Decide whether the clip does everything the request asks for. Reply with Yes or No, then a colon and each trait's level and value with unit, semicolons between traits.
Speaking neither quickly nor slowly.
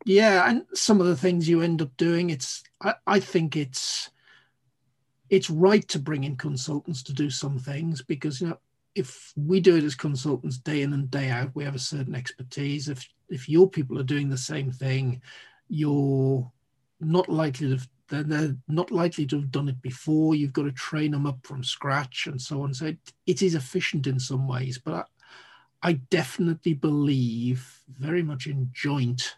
Yes: average, 195 wpm